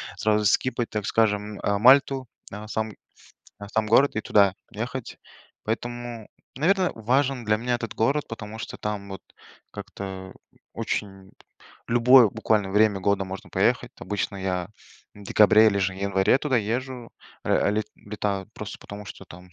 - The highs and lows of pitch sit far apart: No, average, 3.2 semitones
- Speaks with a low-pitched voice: Yes, low, 105 Hz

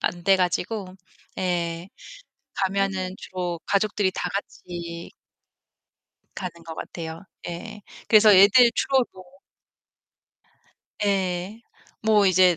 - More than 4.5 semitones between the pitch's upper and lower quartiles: No, narrow, 2.4 semitones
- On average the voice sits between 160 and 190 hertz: Yes, medium, 185 Hz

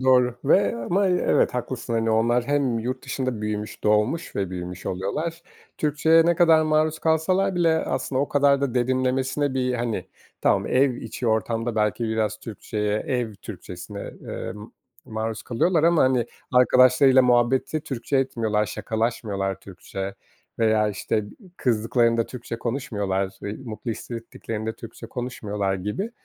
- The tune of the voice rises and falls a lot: No, average, 3.8 semitones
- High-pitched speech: No, low, 120 Hz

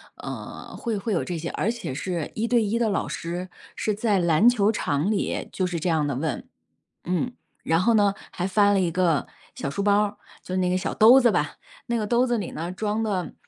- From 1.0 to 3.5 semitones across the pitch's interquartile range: No, average, 4.0 semitones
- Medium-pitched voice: No, high, 195 Hz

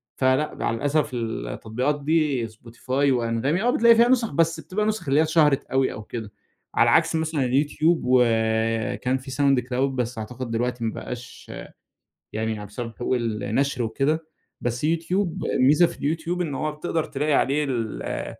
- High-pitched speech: No, low, 135 Hz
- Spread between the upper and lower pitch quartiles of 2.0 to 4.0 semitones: No, average, 4.8 semitones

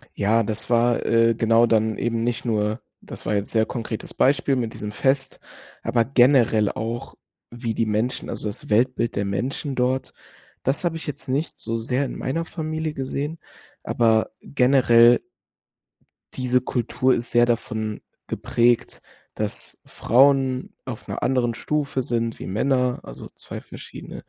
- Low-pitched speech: Yes, low, 120 Hz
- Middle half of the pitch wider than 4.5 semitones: No, average, 2.8 semitones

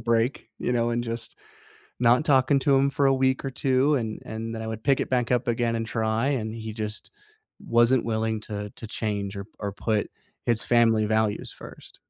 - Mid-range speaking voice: No, low, 115 Hz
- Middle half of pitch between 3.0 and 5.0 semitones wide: No, narrow, 2.6 semitones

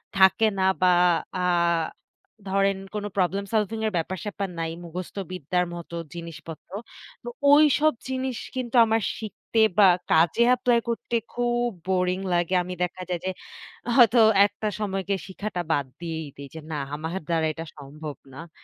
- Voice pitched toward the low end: No, high, 190 Hz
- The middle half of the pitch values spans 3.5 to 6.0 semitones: Yes, average, 4.8 semitones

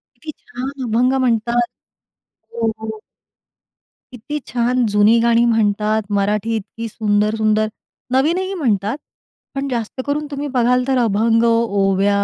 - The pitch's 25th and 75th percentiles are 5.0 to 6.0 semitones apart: No, average, 2.9 semitones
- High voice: Yes, high, 230 Hz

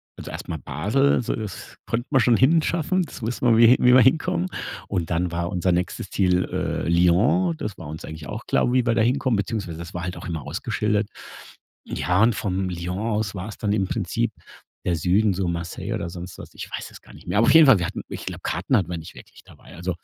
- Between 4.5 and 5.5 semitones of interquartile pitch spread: Yes, average, 5.1 semitones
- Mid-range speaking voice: No, very low, 95 Hz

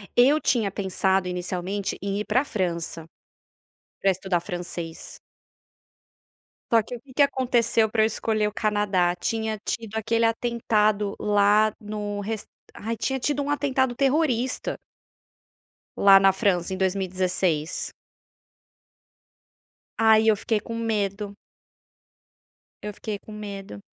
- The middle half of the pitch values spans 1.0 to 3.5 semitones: Yes, average, 3.0 semitones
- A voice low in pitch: No, high, 210 Hz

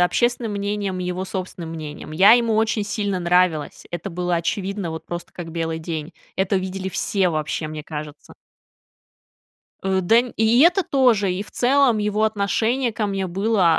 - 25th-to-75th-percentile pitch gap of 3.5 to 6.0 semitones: Yes, average, 4.1 semitones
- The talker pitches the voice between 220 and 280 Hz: No, high, 190 Hz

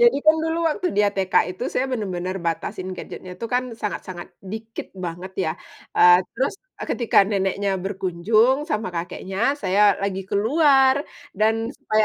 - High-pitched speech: Yes, high, 205 Hz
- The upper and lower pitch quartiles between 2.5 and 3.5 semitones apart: No, average, 4.0 semitones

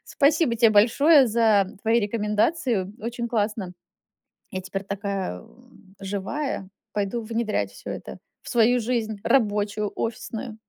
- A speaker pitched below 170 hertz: No, high, 220 Hz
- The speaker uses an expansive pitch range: No, average, 2.7 semitones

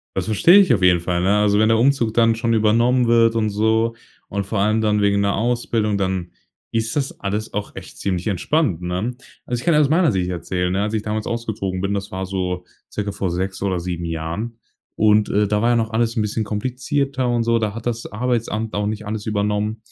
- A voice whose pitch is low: Yes, low, 105 Hz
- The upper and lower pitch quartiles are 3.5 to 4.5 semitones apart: No, average, 2.8 semitones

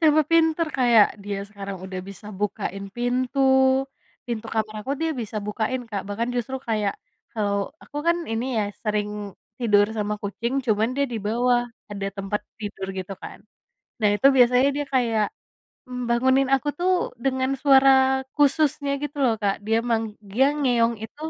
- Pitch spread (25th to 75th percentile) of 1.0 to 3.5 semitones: No, average, 4.3 semitones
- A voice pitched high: Yes, high, 235 Hz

